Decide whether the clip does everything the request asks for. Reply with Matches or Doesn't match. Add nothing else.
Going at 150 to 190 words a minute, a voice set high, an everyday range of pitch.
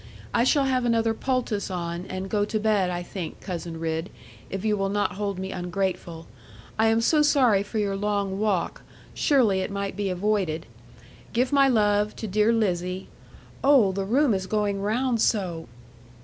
Matches